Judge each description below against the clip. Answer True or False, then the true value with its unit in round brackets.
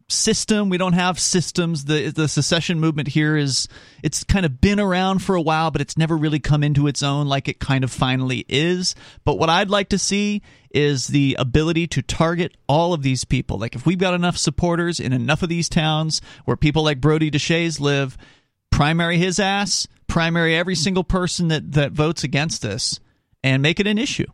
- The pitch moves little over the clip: False (3.9 semitones)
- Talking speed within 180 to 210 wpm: True (200 wpm)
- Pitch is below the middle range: False (155 Hz)